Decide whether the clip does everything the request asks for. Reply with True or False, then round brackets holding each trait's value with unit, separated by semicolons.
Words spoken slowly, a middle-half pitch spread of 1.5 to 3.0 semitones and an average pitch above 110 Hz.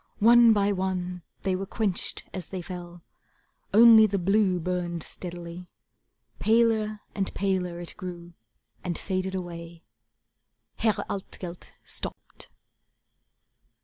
True (110 wpm; 2.7 semitones; 185 Hz)